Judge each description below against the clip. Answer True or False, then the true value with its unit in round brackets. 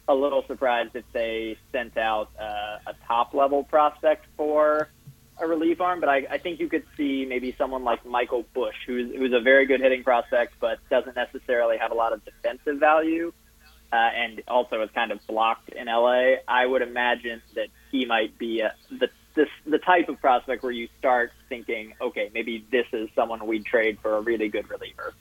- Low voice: True (125 Hz)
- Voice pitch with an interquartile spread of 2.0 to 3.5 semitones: False (4.7 semitones)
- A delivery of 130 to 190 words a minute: False (200 wpm)